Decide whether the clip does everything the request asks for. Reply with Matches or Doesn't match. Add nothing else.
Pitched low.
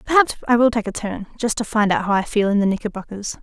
Doesn't match